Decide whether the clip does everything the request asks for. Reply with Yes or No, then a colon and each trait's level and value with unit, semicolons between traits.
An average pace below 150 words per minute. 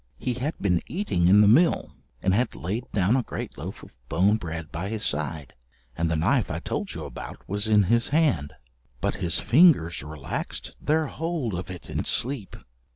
No: average, 190 wpm